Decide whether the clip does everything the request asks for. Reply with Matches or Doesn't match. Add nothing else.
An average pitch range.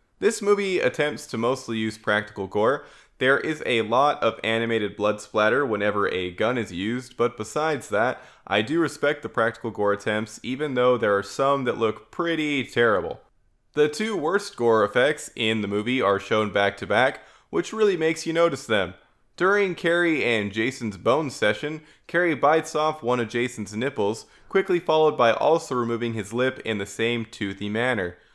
Doesn't match